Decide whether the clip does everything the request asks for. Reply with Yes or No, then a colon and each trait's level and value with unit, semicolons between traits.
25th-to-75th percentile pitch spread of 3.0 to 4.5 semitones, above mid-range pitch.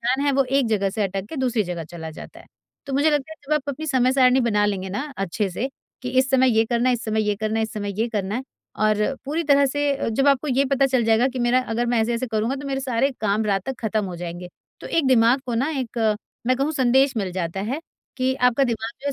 Yes: average, 3.9 semitones; high, 240 Hz